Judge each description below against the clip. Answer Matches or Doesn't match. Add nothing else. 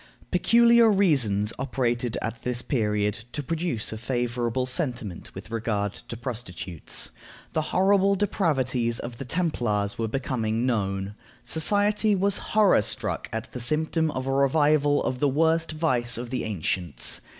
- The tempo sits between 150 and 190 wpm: Doesn't match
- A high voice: Doesn't match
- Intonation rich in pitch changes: Matches